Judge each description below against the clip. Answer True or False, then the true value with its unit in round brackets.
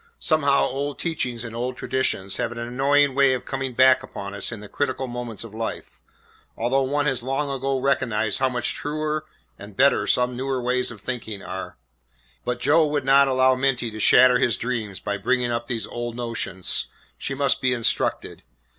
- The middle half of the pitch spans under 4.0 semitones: True (2.6 semitones)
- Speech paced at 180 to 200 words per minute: True (185 wpm)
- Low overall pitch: True (125 Hz)